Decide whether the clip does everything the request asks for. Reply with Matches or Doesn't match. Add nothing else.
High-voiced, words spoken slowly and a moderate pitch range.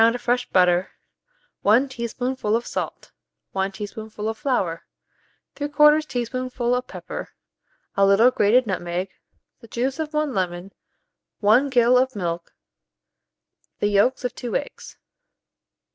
Matches